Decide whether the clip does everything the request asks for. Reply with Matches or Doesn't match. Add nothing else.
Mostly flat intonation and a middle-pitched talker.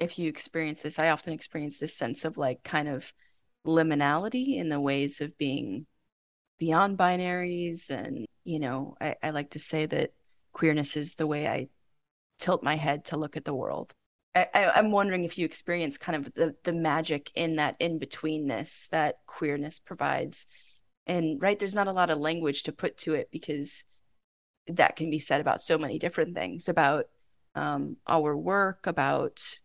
Matches